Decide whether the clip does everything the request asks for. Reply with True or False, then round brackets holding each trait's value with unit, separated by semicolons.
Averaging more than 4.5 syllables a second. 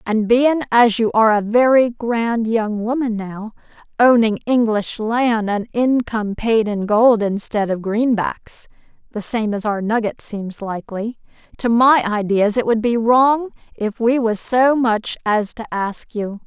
False (4.0 syllables/s)